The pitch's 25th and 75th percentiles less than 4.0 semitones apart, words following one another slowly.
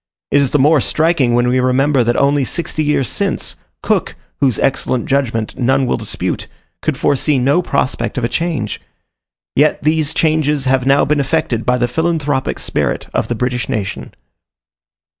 No: average, 3.3 semitones; average, 165 wpm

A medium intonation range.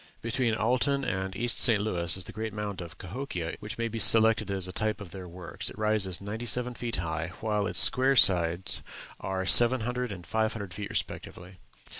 Yes: average, 3.9 semitones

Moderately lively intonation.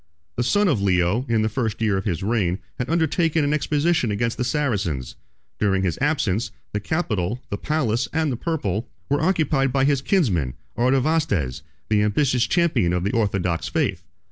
No: wide, 7.1 semitones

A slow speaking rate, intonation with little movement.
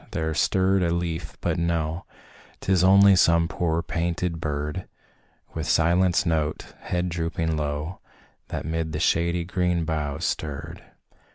Yes: slow, 130 wpm; narrow, 1.9 semitones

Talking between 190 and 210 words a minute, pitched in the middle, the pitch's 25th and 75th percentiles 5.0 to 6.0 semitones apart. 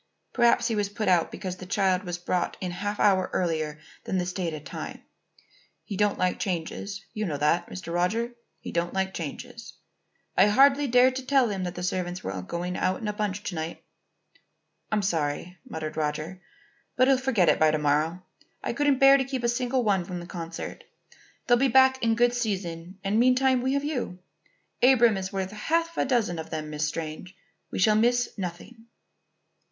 No: average, 195 wpm; high, 195 Hz; wide, 5.6 semitones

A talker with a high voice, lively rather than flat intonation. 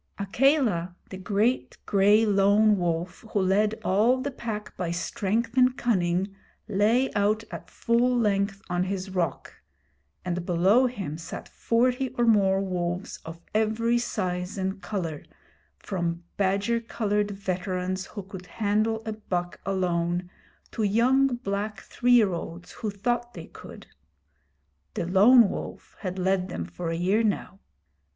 No: high, 200 Hz; average, 3.7 semitones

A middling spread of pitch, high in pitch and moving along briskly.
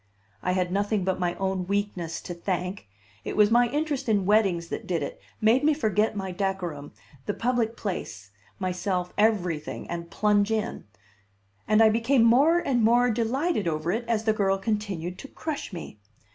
No: average, 4.0 semitones; high, 205 Hz; average, 175 wpm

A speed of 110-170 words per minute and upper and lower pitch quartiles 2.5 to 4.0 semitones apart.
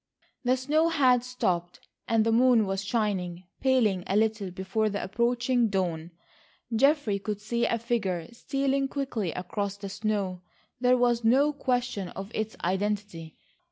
No: average, 145 wpm; average, 4.4 semitones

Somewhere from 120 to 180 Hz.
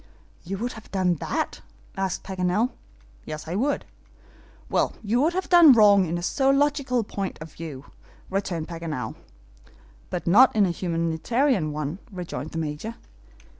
No: high, 190 Hz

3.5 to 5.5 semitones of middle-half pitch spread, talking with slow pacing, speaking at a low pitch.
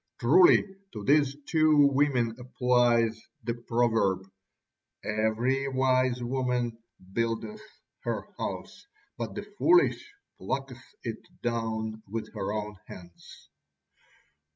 No: average, 3.1 semitones; slow, 100 wpm; low, 120 Hz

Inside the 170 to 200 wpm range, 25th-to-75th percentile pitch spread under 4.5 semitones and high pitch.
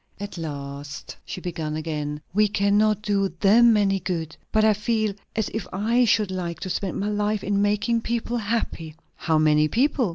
No: average, 175 wpm; average, 4.8 semitones; high, 200 Hz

